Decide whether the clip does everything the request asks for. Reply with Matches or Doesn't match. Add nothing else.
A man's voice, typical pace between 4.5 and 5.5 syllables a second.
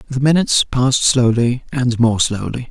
Matches